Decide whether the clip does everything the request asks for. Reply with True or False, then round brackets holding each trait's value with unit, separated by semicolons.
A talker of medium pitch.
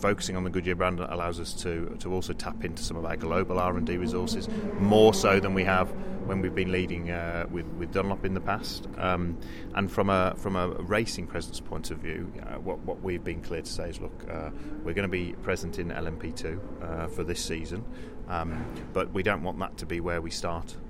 False (90 Hz)